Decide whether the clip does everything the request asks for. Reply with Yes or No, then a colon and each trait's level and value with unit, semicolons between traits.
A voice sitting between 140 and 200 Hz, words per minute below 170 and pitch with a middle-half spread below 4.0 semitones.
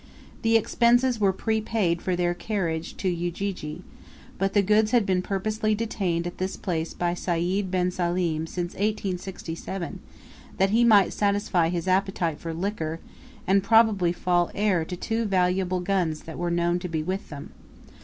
Yes: medium, 185 Hz; average, 160 wpm; average, 2.9 semitones